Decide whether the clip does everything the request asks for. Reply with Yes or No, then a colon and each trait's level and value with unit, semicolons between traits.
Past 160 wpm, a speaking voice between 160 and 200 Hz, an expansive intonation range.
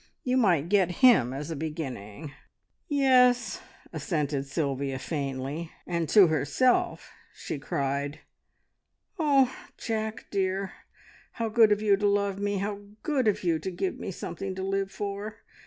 No: average, 140 wpm; high, 190 Hz; wide, 6.2 semitones